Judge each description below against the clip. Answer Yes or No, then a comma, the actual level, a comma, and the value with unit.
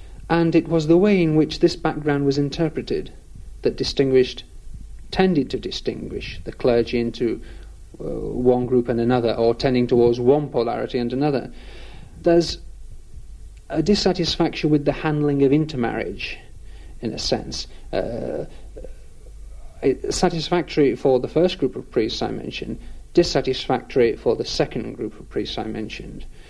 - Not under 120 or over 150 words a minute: Yes, average, 140 wpm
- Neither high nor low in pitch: Yes, medium, 145 Hz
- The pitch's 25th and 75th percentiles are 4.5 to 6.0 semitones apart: Yes, average, 4.9 semitones